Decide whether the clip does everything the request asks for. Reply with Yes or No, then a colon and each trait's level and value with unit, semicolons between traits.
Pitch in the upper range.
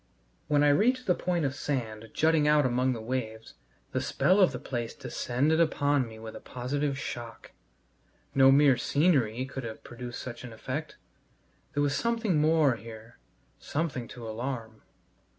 No: low, 135 Hz